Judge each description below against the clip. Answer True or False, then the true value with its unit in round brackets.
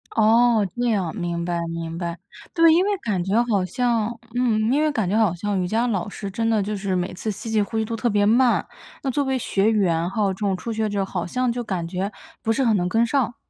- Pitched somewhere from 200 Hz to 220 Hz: True (215 Hz)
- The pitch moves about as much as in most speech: True (3.8 semitones)